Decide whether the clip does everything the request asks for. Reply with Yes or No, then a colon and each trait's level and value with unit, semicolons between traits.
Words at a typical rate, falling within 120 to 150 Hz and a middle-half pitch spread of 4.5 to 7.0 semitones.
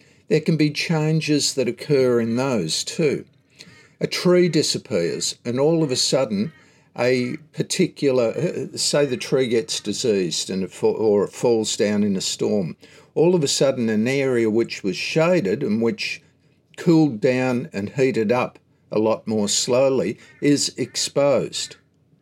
Yes: average, 145 wpm; low, 135 Hz; average, 5.2 semitones